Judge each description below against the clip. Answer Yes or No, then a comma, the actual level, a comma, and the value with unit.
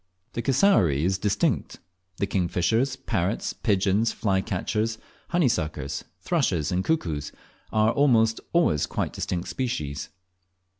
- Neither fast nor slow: No, slow, 105 wpm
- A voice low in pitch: Yes, low, 100 Hz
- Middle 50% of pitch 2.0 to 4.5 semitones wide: No, average, 5.2 semitones